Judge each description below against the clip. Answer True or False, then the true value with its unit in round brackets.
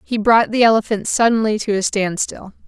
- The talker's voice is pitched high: True (215 Hz)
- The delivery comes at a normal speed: True (180 wpm)